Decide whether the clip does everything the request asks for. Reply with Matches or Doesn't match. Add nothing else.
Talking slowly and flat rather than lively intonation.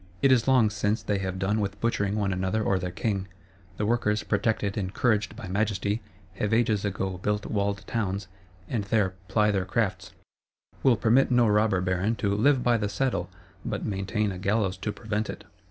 Doesn't match